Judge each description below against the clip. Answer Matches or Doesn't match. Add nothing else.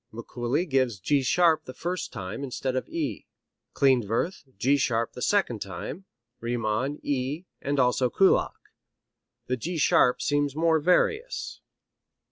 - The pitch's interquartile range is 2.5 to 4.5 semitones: Doesn't match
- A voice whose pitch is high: Doesn't match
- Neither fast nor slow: Doesn't match